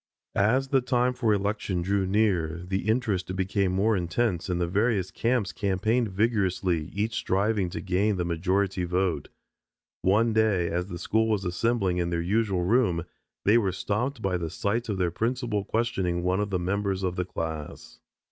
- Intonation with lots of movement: No, average, 3.7 semitones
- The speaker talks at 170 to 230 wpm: Yes, average, 175 wpm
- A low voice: Yes, very low, 95 Hz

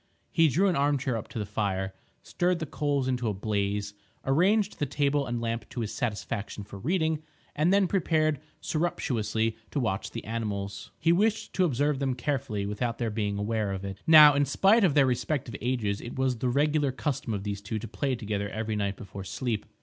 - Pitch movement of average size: No, wide, 6.0 semitones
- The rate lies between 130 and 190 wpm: No, fast, 205 wpm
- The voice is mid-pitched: No, low, 125 Hz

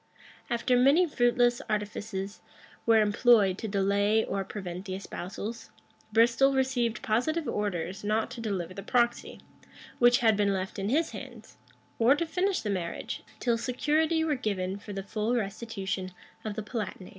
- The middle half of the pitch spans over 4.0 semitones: No, average, 3.7 semitones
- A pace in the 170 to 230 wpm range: No, average, 155 wpm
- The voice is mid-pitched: No, high, 220 Hz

